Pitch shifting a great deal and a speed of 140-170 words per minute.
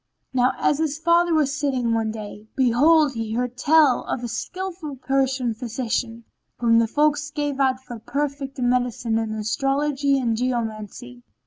No: average, 4.0 semitones; average, 155 wpm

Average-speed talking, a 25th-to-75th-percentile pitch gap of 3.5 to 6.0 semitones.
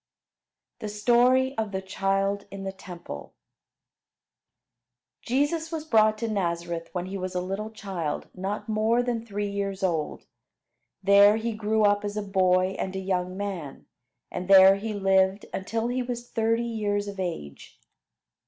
No: average, 155 wpm; average, 2.7 semitones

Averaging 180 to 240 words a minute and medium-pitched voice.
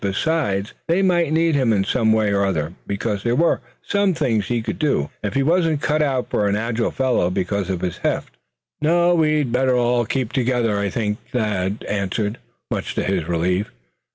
No: average, 190 wpm; low, 115 Hz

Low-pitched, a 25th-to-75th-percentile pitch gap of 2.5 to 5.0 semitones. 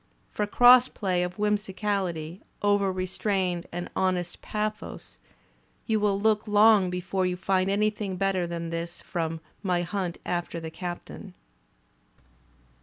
No: high, 190 Hz; average, 2.9 semitones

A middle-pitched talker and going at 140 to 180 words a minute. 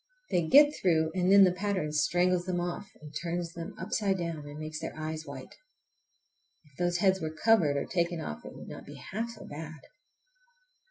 No: medium, 175 Hz; average, 195 wpm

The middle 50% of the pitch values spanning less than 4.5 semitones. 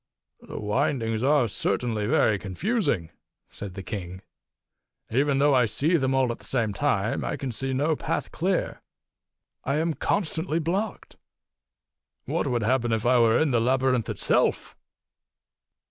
No: average, 4.9 semitones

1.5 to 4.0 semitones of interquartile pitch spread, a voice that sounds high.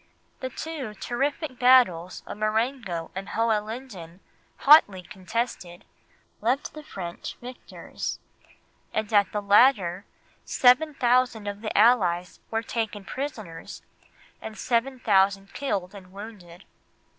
No: average, 4.6 semitones; high, 215 Hz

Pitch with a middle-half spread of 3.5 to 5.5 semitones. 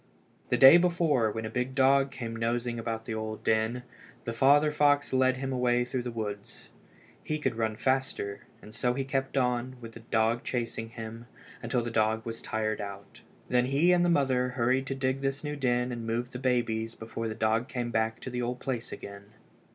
No: average, 2.8 semitones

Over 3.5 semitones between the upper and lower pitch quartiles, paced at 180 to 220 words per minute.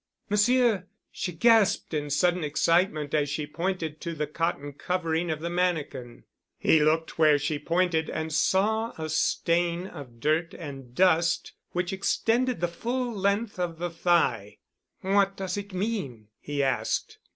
No: average, 4.0 semitones; average, 150 wpm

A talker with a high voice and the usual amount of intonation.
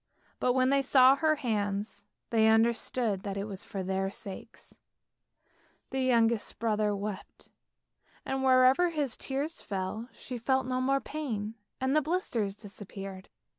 Yes: high, 230 Hz; average, 4.5 semitones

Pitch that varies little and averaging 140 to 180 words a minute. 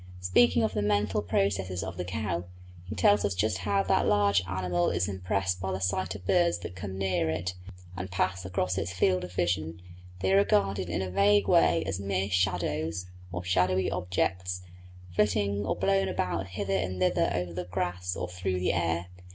No: narrow, 1.5 semitones; average, 190 wpm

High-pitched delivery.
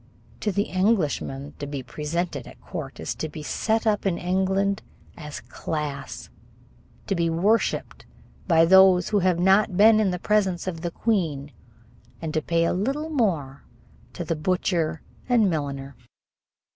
No: medium, 175 Hz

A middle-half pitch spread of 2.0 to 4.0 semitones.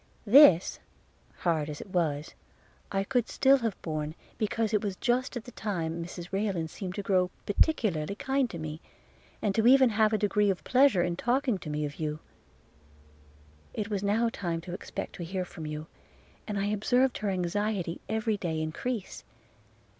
No: average, 4.7 semitones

